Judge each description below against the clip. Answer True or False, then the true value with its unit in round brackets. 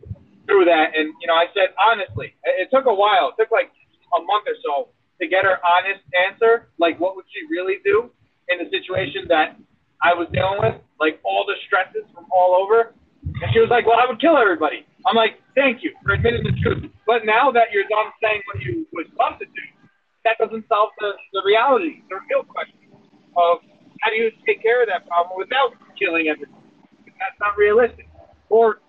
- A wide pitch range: True (6.8 semitones)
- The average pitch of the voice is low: False (220 Hz)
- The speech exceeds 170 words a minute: True (205 wpm)